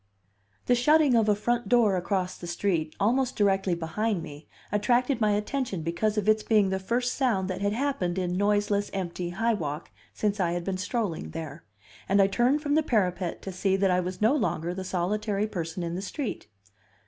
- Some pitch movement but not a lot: Yes, average, 4.0 semitones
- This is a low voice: No, high, 200 Hz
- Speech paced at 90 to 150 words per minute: No, average, 195 wpm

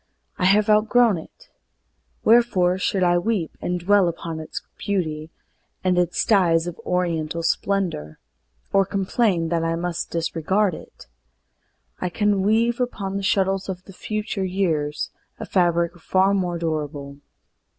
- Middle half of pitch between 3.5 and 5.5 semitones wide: No, average, 3.1 semitones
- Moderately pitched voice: Yes, medium, 180 Hz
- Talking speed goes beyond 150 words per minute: No, average, 140 wpm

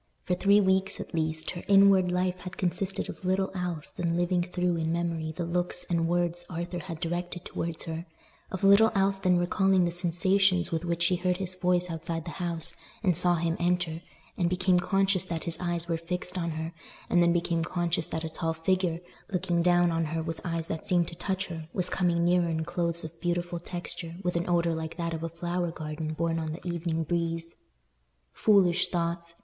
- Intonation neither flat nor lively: No, narrow, 1.5 semitones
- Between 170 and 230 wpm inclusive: Yes, average, 200 wpm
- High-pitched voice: No, medium, 175 Hz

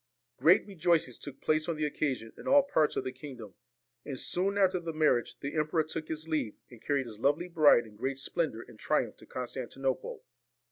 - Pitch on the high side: No, medium, 150 Hz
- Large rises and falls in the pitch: No, average, 4.0 semitones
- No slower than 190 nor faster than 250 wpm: Yes, average, 195 wpm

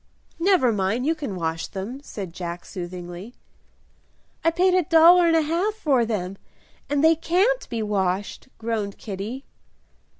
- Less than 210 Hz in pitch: No, high, 235 Hz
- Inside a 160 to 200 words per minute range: No, average, 145 wpm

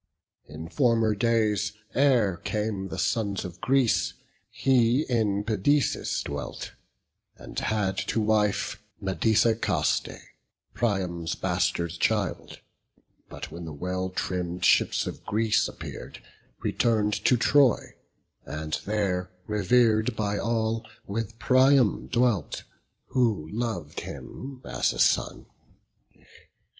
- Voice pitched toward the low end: Yes, low, 105 Hz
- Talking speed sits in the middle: No, slow, 105 wpm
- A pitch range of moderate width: Yes, average, 4.0 semitones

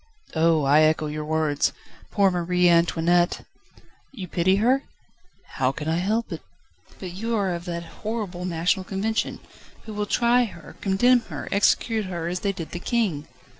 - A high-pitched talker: No, medium, 180 Hz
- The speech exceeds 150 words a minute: Yes, average, 160 wpm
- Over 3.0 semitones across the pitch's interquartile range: Yes, average, 4.1 semitones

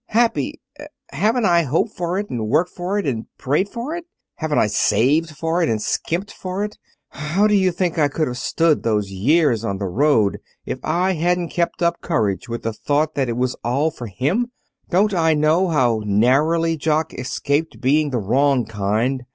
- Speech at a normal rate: Yes, average, 190 wpm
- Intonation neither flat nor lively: No, wide, 6.2 semitones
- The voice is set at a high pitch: No, medium, 155 Hz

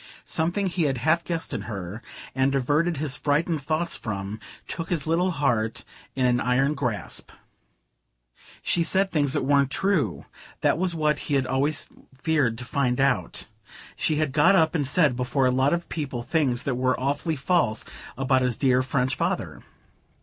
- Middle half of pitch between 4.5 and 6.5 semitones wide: No, average, 4.0 semitones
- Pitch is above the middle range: No, medium, 140 Hz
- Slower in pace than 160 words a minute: No, average, 170 wpm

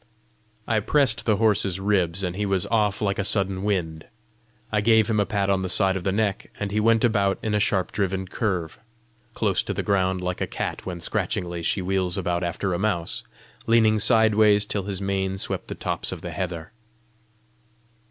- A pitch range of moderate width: No, narrow, 2.3 semitones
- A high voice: No, low, 100 Hz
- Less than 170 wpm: No, average, 195 wpm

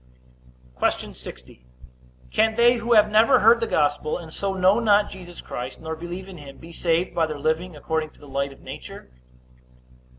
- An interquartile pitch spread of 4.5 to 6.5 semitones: Yes, average, 5.2 semitones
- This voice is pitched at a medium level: Yes, medium, 175 Hz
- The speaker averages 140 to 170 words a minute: No, average, 185 wpm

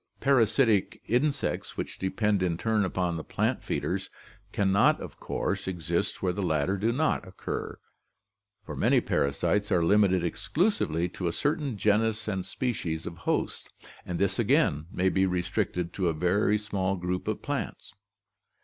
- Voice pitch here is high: No, very low, 95 Hz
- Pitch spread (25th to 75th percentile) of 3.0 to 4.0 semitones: Yes, average, 3.5 semitones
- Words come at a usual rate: Yes, average, 160 wpm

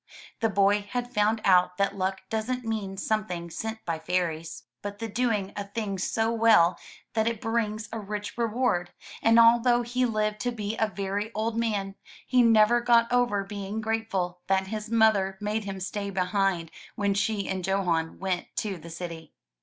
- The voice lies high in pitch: Yes, high, 210 Hz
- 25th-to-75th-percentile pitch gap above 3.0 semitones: No, average, 2.7 semitones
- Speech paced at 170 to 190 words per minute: Yes, average, 175 wpm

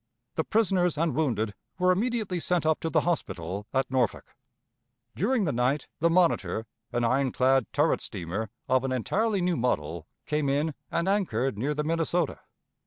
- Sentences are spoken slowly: No, average, 165 wpm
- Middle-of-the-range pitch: Yes, medium, 150 Hz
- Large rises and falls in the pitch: Yes, wide, 6.1 semitones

